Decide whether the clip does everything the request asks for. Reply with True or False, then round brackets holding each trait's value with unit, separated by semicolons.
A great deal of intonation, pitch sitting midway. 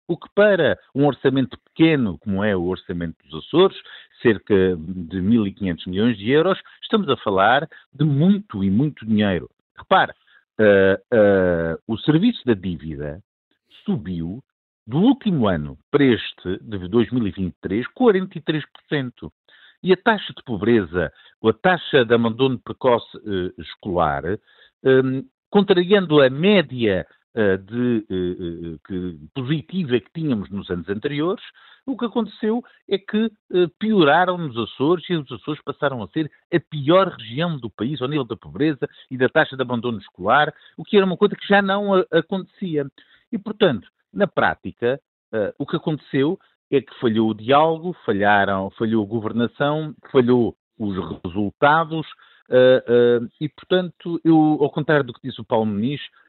False (8.5 semitones; 130 Hz)